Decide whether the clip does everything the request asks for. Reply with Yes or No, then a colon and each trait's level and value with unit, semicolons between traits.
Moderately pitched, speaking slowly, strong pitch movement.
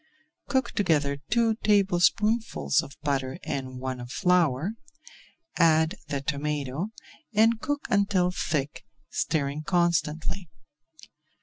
Yes: medium, 160 Hz; slow, 100 wpm; wide, 6.0 semitones